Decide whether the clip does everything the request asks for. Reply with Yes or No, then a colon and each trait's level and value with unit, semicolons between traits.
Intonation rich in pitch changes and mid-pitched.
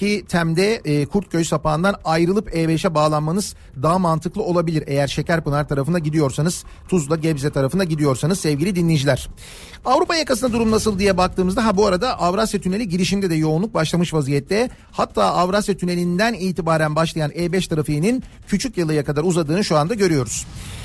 No: average, 4.4 semitones; medium, 175 Hz